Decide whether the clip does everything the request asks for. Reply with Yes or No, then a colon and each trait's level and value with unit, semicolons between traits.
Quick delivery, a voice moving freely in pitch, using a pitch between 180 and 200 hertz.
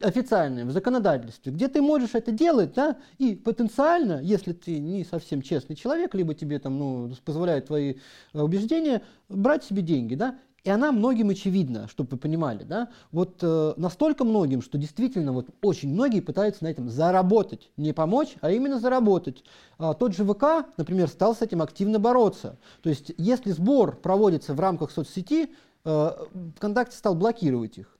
Yes: fast, 165 wpm; wide, 7.6 semitones; high, 190 Hz